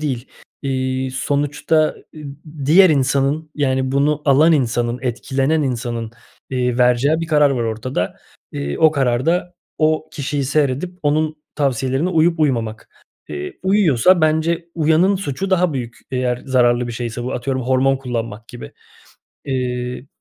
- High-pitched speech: No, low, 135 Hz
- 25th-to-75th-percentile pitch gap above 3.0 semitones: Yes, average, 4.0 semitones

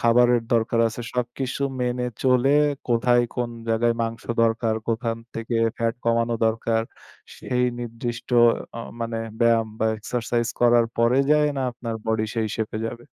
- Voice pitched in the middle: No, low, 115 Hz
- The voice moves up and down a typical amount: No, narrow, 1.2 semitones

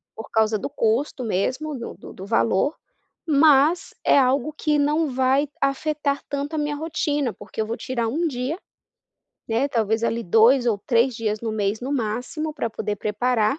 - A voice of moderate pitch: No, very high, 255 Hz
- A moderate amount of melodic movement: Yes, average, 4.7 semitones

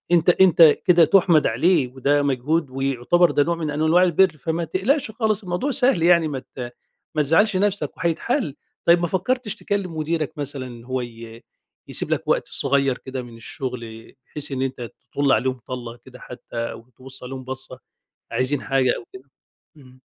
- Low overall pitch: No, medium, 145 Hz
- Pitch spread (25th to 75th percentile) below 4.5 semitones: No, average, 5.3 semitones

